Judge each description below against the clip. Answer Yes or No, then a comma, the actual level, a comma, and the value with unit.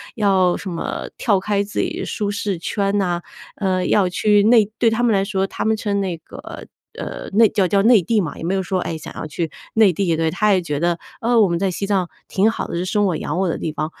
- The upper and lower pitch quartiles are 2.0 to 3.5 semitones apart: Yes, average, 2.9 semitones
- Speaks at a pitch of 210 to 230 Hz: No, high, 195 Hz